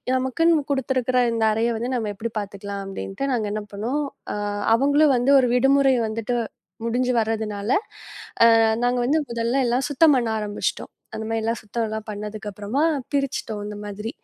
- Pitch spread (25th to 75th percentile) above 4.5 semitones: No, average, 3.6 semitones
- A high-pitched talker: Yes, high, 230 Hz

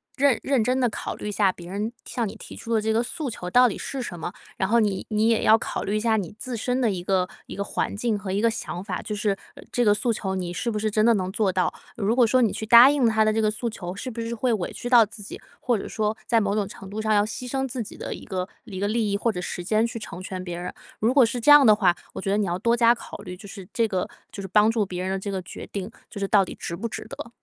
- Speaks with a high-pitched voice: Yes, high, 215 Hz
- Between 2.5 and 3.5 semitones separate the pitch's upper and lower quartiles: Yes, average, 3.2 semitones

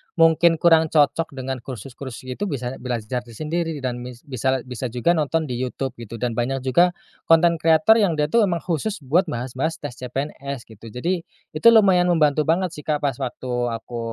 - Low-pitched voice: No, medium, 145 Hz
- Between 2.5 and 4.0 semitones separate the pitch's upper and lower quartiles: No, average, 4.7 semitones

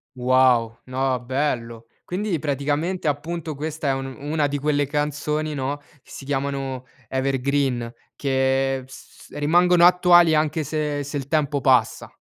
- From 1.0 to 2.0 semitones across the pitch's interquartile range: No, narrow, 2.5 semitones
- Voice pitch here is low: No, medium, 145 Hz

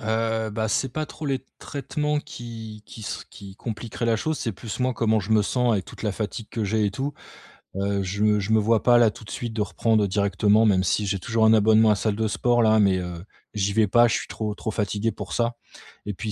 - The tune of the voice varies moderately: No, narrow, 2.2 semitones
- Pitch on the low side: Yes, low, 110 Hz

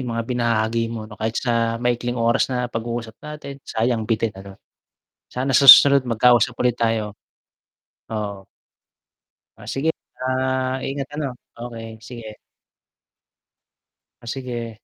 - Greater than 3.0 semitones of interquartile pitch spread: No, narrow, 2.4 semitones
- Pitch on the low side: Yes, low, 120 Hz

